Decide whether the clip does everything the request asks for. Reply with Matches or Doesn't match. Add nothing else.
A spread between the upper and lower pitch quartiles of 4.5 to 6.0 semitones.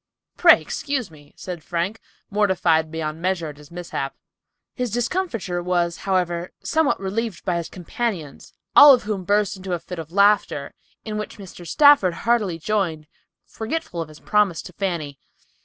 Doesn't match